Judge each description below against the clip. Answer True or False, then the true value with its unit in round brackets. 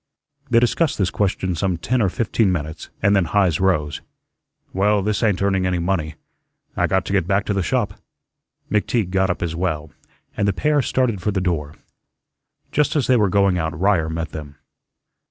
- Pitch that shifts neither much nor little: True (3.3 semitones)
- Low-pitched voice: True (95 Hz)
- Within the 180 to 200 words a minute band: True (190 wpm)